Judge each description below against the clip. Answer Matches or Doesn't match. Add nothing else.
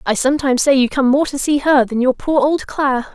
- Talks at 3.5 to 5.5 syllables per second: Doesn't match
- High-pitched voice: Matches